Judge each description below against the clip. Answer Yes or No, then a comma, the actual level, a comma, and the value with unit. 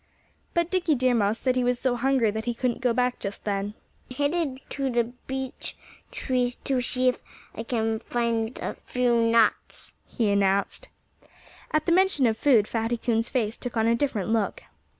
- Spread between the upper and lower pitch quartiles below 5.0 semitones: Yes, narrow, 2.5 semitones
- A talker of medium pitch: No, high, 240 Hz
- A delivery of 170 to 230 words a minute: Yes, average, 190 wpm